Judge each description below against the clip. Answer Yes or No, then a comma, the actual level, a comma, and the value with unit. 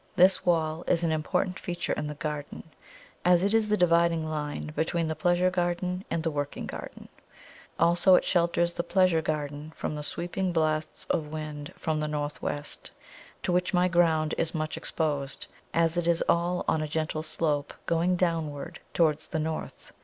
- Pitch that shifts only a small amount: Yes, narrow, 2.3 semitones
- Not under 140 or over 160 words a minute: No, average, 175 wpm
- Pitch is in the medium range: Yes, medium, 165 Hz